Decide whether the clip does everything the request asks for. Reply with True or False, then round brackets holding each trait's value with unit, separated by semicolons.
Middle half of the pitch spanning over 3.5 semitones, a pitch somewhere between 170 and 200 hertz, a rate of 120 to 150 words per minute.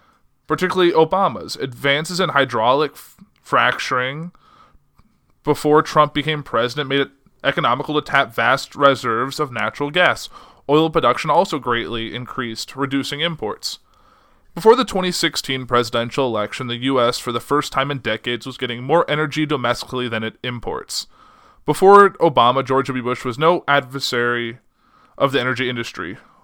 False (4.1 semitones; 140 Hz; 140 wpm)